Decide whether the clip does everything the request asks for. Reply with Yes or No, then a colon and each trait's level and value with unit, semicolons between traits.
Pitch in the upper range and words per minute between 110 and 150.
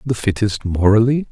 No: low, 110 Hz; slow, 135 wpm